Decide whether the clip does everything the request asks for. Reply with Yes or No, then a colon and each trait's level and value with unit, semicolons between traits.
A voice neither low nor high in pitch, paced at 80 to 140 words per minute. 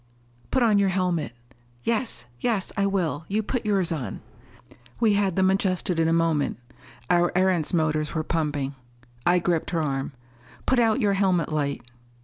No: medium, 180 Hz; average, 155 wpm